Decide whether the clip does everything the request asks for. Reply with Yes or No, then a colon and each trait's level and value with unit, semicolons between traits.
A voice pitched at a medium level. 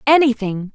No: high, 240 Hz